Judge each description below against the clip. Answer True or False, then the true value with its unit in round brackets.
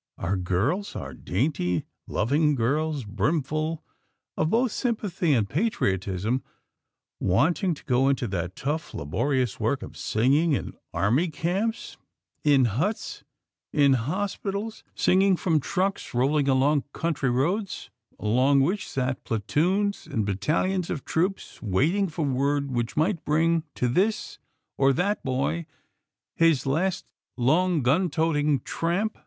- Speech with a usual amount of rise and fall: False (5.9 semitones)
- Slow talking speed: True (125 wpm)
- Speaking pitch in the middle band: True (150 Hz)